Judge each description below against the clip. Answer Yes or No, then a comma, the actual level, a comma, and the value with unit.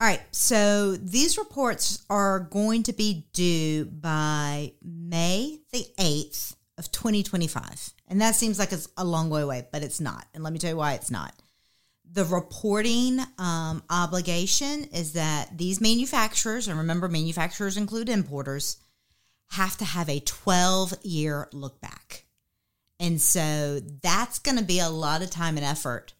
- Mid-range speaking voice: Yes, medium, 175 Hz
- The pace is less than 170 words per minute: Yes, average, 160 wpm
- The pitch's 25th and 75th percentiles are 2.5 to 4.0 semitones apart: No, average, 5.1 semitones